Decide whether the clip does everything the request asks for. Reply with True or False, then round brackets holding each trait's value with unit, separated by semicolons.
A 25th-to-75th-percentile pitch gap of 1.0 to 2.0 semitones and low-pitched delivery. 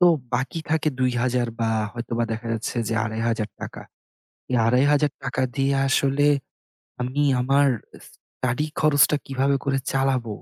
False (2.8 semitones; 130 Hz)